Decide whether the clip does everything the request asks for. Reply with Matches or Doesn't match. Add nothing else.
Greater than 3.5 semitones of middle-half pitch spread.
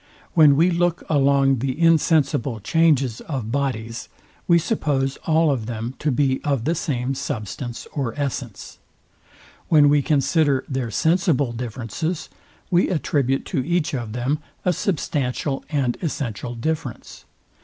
Matches